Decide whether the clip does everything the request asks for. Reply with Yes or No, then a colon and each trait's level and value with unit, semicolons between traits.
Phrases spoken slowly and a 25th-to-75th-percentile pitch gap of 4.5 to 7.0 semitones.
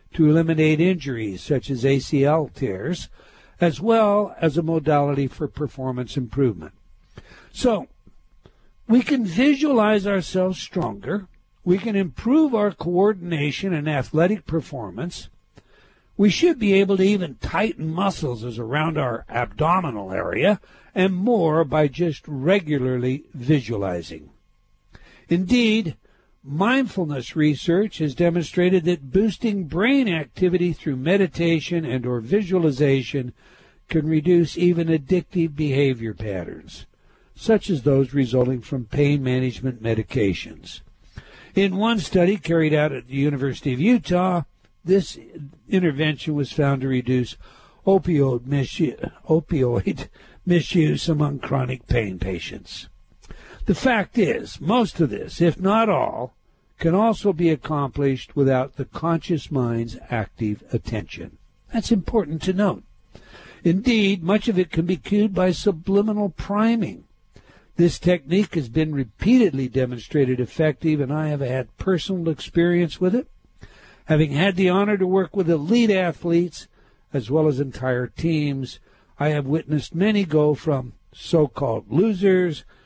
Yes: slow, 125 wpm; wide, 5.6 semitones